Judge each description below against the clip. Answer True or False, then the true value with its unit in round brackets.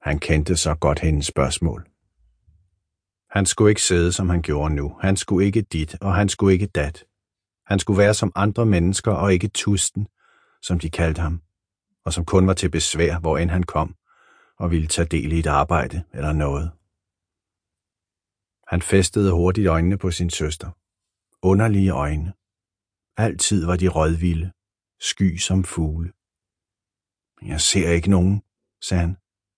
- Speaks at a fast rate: False (155 wpm)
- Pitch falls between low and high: False (90 Hz)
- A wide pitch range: False (2.7 semitones)